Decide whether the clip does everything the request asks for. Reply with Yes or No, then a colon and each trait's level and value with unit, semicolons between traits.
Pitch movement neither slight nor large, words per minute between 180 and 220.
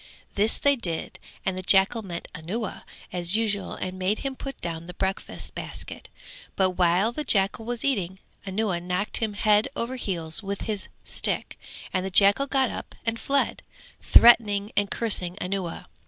No: average, 3.7 semitones; average, 165 wpm